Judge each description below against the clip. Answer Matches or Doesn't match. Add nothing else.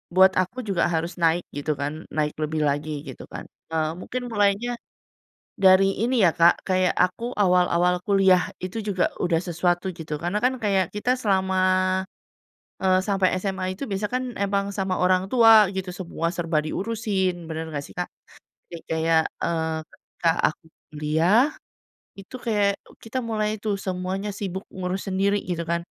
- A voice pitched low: Doesn't match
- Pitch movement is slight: Doesn't match